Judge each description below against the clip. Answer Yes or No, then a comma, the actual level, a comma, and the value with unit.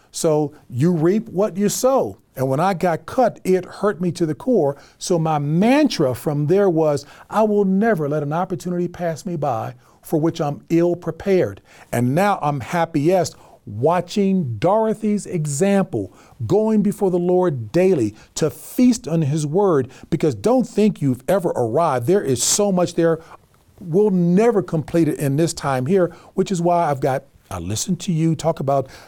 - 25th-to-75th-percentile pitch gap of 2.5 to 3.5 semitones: No, average, 4.6 semitones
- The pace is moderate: Yes, average, 175 wpm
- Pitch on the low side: No, medium, 170 Hz